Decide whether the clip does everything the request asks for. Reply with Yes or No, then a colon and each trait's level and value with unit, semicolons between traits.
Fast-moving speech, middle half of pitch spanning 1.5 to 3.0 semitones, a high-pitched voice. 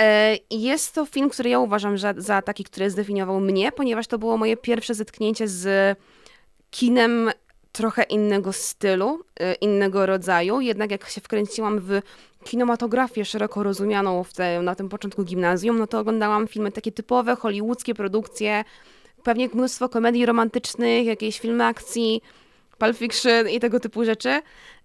No: average, 140 wpm; average, 2.7 semitones; high, 220 Hz